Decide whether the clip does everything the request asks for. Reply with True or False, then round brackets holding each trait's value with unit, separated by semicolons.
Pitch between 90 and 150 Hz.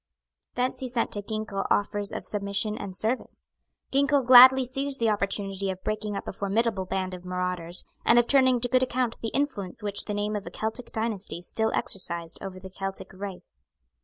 False (210 Hz)